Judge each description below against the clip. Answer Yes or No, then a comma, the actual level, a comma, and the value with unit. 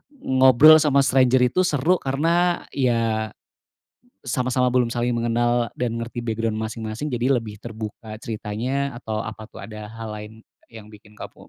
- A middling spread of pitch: Yes, average, 3.1 semitones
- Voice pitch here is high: No, low, 120 Hz